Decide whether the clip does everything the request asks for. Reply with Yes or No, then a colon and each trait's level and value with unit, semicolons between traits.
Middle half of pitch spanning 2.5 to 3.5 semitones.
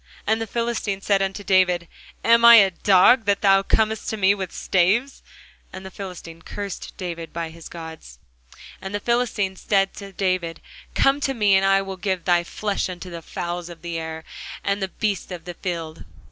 Yes: average, 2.9 semitones